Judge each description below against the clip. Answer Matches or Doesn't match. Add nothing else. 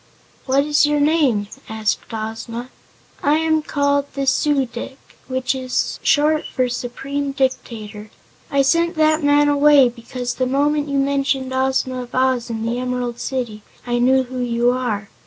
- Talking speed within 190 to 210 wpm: Doesn't match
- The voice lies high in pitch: Matches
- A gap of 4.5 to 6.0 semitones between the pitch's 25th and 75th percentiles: Doesn't match